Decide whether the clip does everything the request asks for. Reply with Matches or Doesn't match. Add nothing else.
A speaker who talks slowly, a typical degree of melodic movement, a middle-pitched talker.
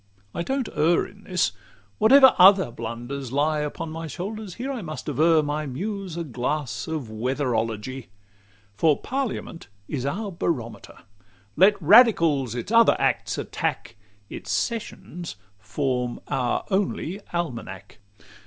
Doesn't match